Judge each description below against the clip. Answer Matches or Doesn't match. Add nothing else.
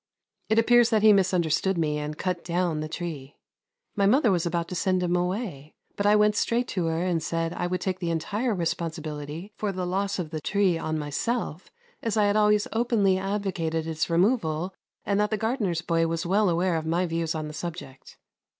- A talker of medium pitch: Matches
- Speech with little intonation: Doesn't match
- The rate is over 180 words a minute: Matches